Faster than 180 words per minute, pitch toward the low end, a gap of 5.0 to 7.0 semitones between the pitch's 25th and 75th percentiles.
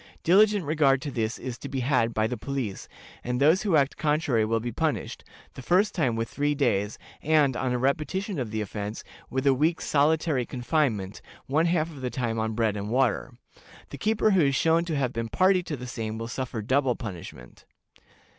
Yes: average, 200 wpm; low, 130 Hz; average, 5.3 semitones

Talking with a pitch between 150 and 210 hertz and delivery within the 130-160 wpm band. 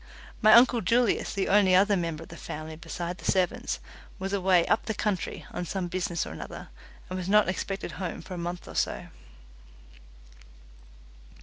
No: medium, 185 Hz; average, 175 wpm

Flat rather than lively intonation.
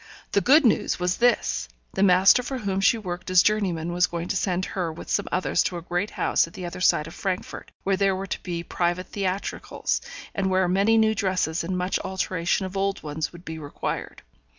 Yes: narrow, 2.2 semitones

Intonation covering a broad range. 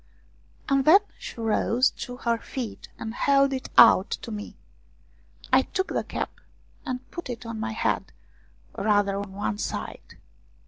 No: average, 3.8 semitones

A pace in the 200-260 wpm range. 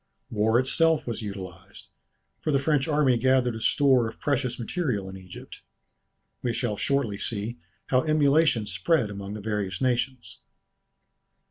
No: average, 140 wpm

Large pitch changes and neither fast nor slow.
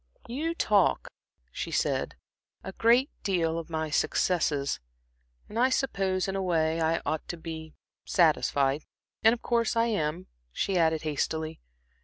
Yes: wide, 6.0 semitones; average, 145 wpm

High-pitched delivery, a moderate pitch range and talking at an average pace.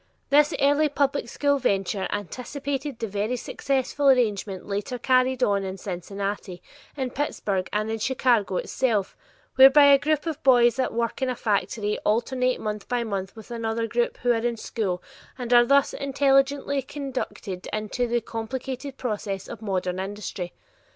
Yes: high, 235 Hz; average, 4.6 semitones; average, 155 wpm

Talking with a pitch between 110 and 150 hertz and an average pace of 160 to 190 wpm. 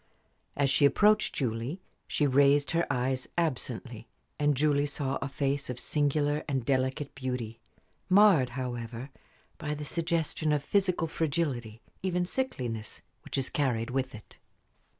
No: medium, 140 Hz; slow, 135 wpm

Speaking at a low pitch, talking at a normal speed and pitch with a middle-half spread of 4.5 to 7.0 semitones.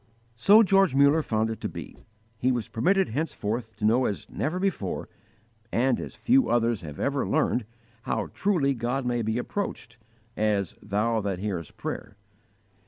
Yes: low, 120 Hz; average, 160 wpm; average, 4.9 semitones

